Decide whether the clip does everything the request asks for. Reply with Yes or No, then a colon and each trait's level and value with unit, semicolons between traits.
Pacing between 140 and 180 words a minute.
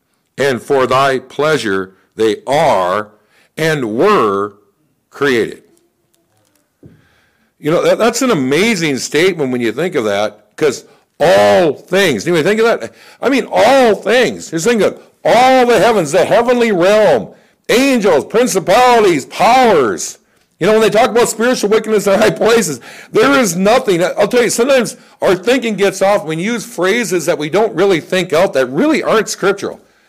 Yes: average, 160 wpm